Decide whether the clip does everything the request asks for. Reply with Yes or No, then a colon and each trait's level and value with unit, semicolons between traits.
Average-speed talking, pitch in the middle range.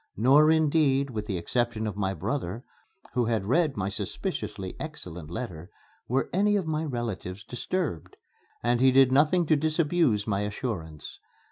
No: average, 150 wpm; low, 120 Hz